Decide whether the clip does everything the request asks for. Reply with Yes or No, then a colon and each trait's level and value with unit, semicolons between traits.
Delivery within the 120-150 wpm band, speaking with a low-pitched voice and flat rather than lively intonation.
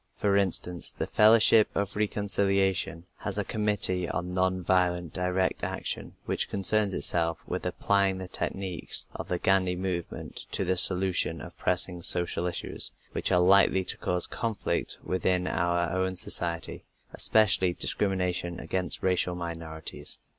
Yes: average, 140 wpm; very low, 90 Hz; narrow, 1.8 semitones